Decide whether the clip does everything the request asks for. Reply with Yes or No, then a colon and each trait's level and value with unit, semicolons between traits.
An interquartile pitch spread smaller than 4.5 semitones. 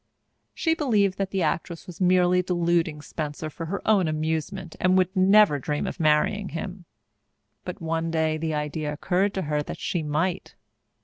Yes: average, 3.2 semitones